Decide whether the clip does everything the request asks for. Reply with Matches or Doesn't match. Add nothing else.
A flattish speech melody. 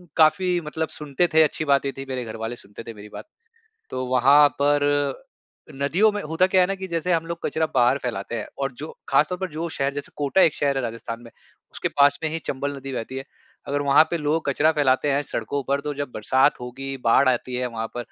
Doesn't match